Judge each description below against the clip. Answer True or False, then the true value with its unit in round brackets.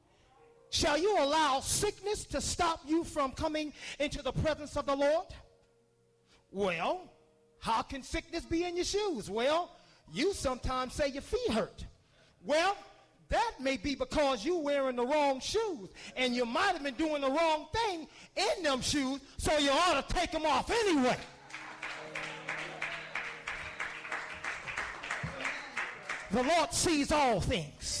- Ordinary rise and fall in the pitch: True (4.2 semitones)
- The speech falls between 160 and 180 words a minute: False (140 wpm)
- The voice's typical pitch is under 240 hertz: False (300 Hz)